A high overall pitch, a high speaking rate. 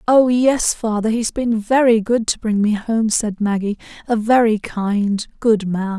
No: high, 220 Hz; average, 170 wpm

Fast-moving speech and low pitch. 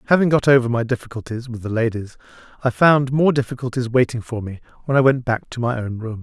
Yes: fast, 220 wpm; low, 125 Hz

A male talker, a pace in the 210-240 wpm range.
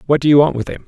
No: male; fast, 410 wpm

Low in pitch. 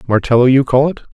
Yes: low, 130 Hz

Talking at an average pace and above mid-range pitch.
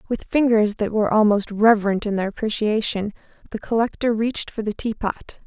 Yes: average, 165 wpm; high, 215 Hz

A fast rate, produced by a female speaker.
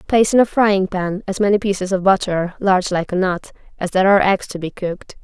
Yes: fast, 240 wpm; female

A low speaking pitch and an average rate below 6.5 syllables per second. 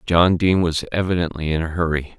Yes: very low, 85 Hz; 5.9 syllables/s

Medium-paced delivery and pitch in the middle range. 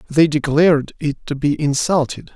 Yes: average, 155 wpm; medium, 150 Hz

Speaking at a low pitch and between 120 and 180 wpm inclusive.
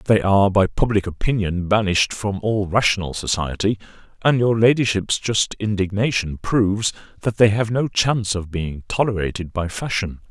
Yes: low, 100 Hz; average, 150 wpm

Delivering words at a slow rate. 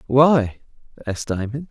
Yes: slow, 105 wpm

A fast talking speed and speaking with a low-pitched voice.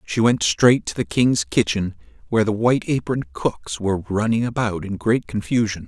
No: average, 185 wpm; low, 105 Hz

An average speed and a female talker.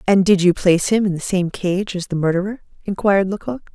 No: fast, 225 wpm; female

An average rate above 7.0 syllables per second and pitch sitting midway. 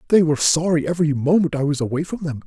Yes: 7.2 syllables/s; medium, 155 Hz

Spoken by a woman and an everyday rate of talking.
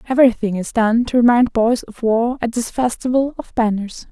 Yes: female; average, 190 wpm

